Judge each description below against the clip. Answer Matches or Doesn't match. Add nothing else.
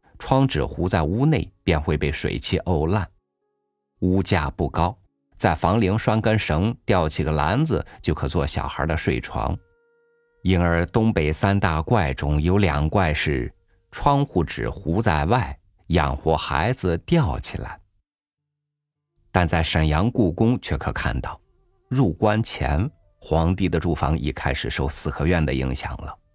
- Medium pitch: Doesn't match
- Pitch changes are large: Matches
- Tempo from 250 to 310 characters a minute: Doesn't match